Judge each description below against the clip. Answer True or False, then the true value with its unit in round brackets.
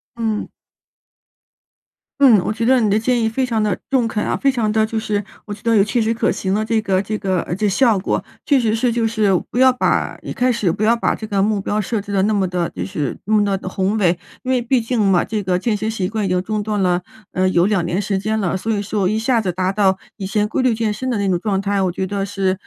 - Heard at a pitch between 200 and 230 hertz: True (210 Hz)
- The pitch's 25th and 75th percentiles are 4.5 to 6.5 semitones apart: False (2.8 semitones)